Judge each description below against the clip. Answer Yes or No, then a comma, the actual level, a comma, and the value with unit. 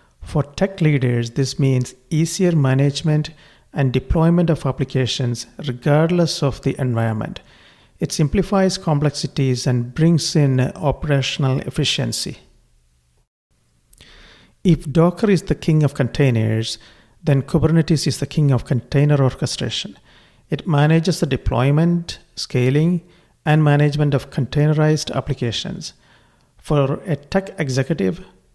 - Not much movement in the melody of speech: No, average, 3.7 semitones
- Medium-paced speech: No, slow, 110 wpm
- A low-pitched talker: No, medium, 145 Hz